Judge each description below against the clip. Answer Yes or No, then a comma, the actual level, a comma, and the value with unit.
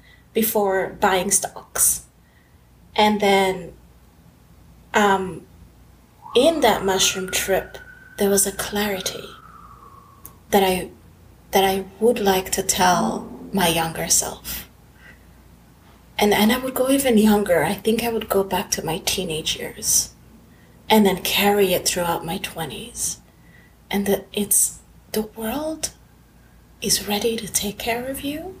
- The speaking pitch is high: Yes, high, 200 Hz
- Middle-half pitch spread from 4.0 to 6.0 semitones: No, average, 3.0 semitones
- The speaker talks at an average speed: No, slow, 130 wpm